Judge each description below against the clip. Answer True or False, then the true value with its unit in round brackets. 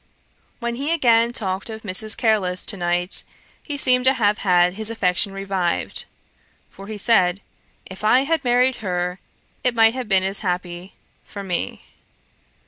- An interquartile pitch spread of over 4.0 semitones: True (4.5 semitones)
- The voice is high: True (205 Hz)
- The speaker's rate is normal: True (155 wpm)